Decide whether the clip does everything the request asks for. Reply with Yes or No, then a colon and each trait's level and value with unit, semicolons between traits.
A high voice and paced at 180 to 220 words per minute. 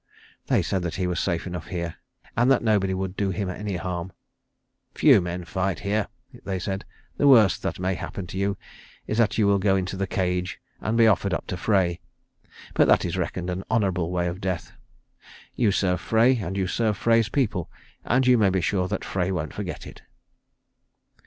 No: very low, 95 Hz; average, 195 wpm